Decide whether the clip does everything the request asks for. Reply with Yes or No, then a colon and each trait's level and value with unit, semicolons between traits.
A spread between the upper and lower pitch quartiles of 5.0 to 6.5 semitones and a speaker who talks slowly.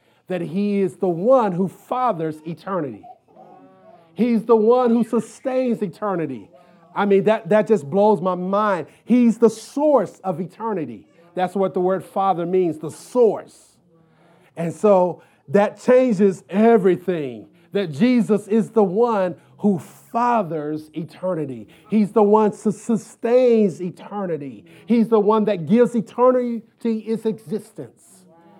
No: average, 4.6 semitones; slow, 130 wpm